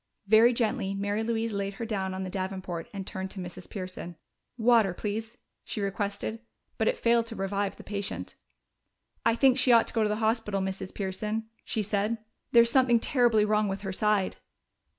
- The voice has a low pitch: No, high, 210 Hz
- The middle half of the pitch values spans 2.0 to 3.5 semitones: Yes, average, 2.9 semitones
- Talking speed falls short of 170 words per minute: No, average, 185 wpm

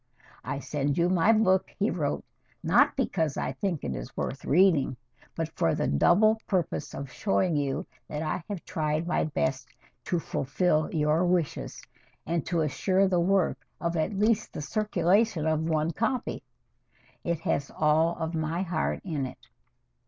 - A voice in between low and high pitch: Yes, medium, 165 Hz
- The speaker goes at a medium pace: Yes, average, 160 wpm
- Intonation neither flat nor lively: Yes, average, 3.7 semitones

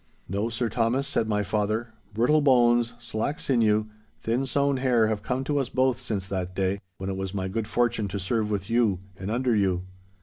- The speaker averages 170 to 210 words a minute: Yes, average, 200 wpm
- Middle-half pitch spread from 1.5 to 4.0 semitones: Yes, average, 3.5 semitones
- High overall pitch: No, low, 115 Hz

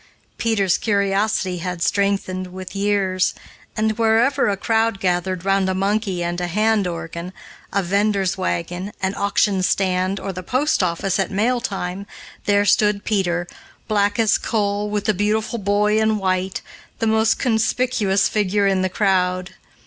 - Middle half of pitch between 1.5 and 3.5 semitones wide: Yes, narrow, 2.4 semitones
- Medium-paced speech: Yes, average, 150 wpm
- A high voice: Yes, high, 200 Hz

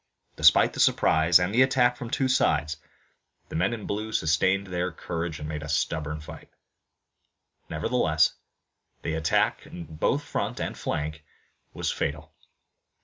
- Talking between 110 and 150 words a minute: Yes, average, 145 wpm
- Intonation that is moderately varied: Yes, average, 4.7 semitones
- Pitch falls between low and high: No, very low, 80 Hz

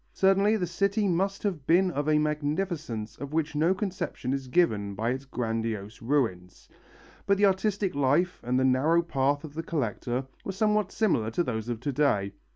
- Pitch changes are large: Yes, wide, 6.7 semitones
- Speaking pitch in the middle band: Yes, medium, 150 Hz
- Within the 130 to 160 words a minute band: No, average, 180 wpm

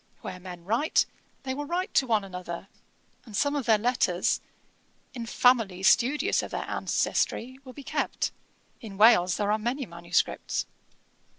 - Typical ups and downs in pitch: No, wide, 5.7 semitones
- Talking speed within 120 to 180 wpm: Yes, average, 155 wpm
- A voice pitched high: Yes, high, 225 Hz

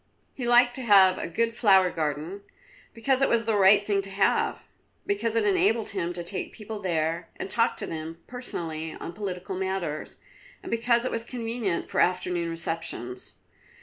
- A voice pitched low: No, high, 195 Hz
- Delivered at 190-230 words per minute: No, average, 175 wpm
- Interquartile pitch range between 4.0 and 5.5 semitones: Yes, average, 5.1 semitones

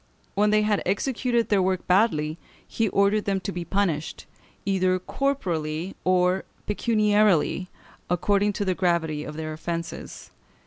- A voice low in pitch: No, high, 190 Hz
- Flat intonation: No, average, 3.4 semitones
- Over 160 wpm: No, slow, 135 wpm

